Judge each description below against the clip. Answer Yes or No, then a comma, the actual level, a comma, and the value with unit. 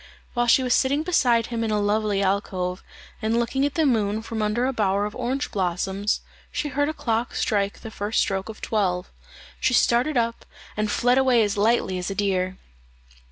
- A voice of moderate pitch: No, high, 220 Hz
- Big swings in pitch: No, average, 3.4 semitones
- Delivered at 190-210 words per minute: Yes, average, 195 wpm